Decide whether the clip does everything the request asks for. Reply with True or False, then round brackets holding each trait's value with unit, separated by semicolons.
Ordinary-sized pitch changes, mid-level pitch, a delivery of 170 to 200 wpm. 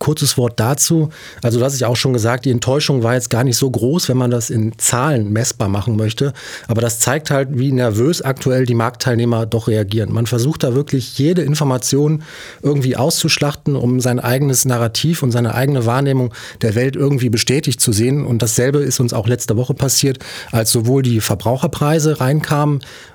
False (3.1 semitones; 125 Hz; 190 wpm)